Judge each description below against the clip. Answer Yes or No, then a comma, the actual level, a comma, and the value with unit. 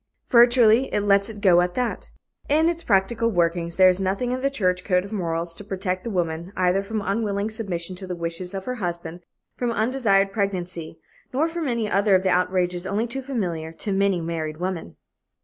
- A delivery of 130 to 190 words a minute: No, average, 200 wpm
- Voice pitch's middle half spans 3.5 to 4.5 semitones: Yes, average, 4.0 semitones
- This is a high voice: Yes, high, 195 Hz